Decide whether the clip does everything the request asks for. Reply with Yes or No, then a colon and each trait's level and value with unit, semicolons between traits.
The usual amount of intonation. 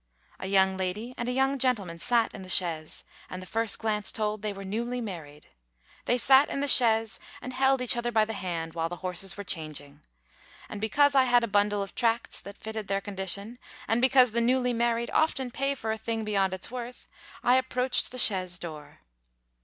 Yes: average, 4.5 semitones